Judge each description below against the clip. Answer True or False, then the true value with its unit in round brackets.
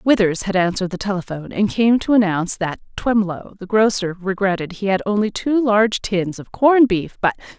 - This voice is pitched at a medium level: False (200 Hz)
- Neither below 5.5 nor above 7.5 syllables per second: True (5.6 syllables/s)